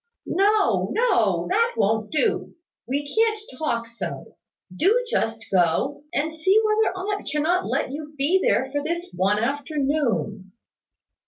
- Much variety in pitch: Yes, wide, 8.7 semitones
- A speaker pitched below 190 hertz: No, very high, 300 Hz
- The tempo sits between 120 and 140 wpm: Yes, slow, 135 wpm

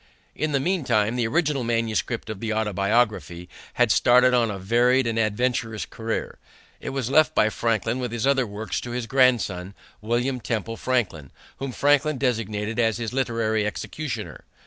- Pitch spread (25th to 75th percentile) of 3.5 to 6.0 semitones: No, average, 2.8 semitones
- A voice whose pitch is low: Yes, low, 115 Hz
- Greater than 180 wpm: No, average, 160 wpm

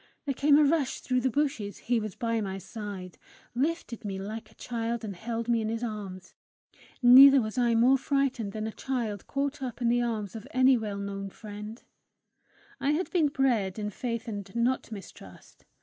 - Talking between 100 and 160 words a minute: No, average, 190 wpm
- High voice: Yes, high, 230 Hz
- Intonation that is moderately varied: Yes, average, 3.8 semitones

